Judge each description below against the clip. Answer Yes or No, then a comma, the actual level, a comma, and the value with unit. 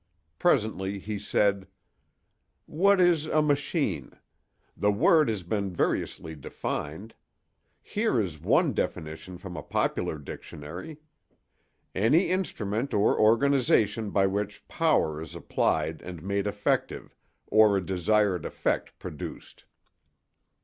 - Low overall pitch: Yes, low, 105 Hz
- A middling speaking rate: No, slow, 110 wpm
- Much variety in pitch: Yes, wide, 6.6 semitones